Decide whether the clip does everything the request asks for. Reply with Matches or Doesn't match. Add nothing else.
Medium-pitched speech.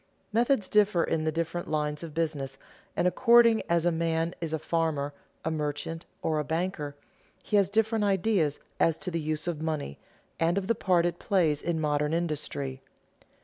Matches